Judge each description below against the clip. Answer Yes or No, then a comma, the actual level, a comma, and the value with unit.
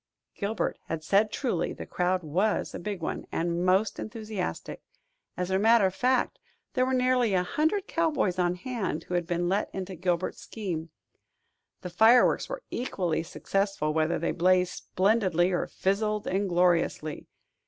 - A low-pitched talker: No, high, 190 Hz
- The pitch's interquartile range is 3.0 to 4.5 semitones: Yes, average, 3.8 semitones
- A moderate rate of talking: Yes, average, 155 wpm